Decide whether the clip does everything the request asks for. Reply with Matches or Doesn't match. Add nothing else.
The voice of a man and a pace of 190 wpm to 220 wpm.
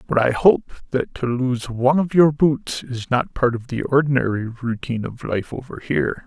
Matches